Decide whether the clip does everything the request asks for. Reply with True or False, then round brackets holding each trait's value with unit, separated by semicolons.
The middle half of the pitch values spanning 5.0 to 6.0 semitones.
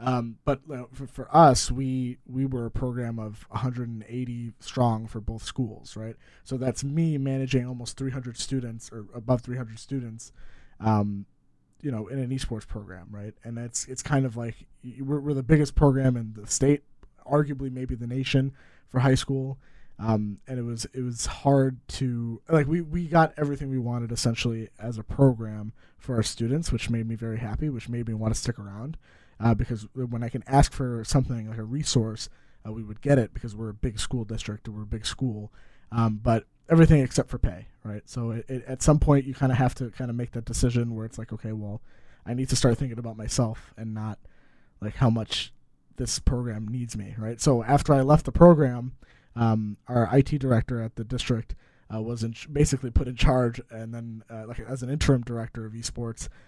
False (3.0 semitones)